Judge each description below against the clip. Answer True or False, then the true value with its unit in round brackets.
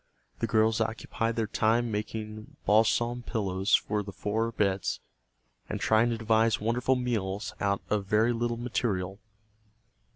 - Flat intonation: True (1.9 semitones)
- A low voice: True (110 Hz)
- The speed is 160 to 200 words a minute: False (135 wpm)